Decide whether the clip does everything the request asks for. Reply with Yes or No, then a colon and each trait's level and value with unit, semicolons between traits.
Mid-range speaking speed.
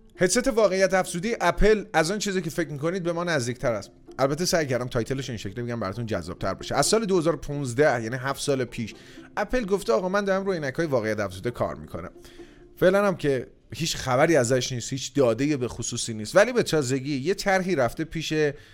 No: fast, 200 wpm